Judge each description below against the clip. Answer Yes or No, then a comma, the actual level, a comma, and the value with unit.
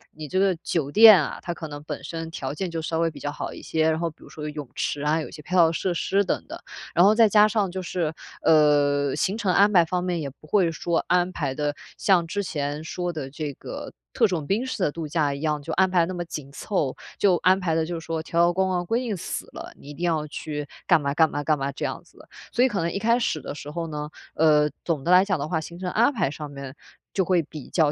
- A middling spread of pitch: Yes, average, 3.6 semitones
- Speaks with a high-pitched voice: No, medium, 165 Hz